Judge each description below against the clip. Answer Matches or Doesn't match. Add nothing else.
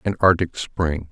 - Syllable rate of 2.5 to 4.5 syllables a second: Matches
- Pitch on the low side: Matches